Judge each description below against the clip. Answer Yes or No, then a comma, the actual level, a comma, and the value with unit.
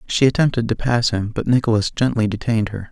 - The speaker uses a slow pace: No, fast, 205 wpm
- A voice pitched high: No, low, 115 Hz